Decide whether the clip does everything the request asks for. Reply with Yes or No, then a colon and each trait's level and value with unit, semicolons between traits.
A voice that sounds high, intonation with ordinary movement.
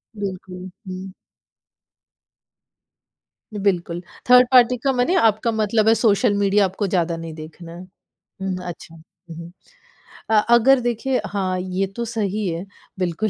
Yes: high, 200 Hz; average, 3.8 semitones